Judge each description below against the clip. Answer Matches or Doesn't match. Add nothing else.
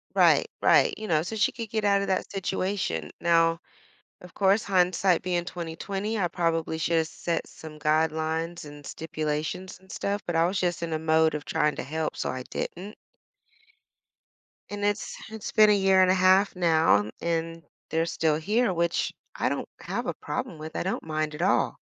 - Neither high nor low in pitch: Matches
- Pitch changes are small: Doesn't match